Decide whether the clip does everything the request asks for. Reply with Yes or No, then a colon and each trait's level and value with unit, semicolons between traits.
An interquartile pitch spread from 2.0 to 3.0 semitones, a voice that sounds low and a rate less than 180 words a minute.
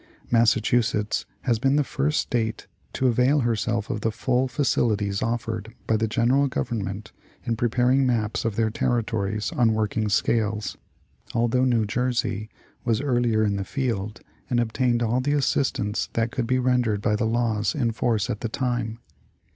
Yes: narrow, 2.4 semitones; low, 115 Hz; average, 165 wpm